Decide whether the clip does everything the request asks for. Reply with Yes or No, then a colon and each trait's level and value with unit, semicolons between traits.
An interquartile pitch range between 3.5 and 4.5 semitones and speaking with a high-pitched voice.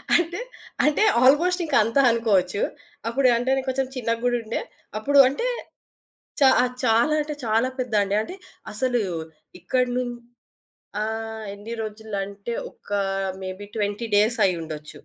Yes: average, 3.9 semitones; high, 230 Hz